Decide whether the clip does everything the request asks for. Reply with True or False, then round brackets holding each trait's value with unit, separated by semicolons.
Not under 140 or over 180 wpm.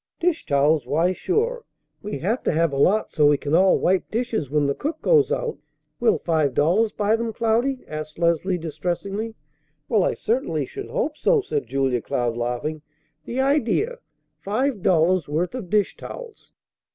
True (170 wpm)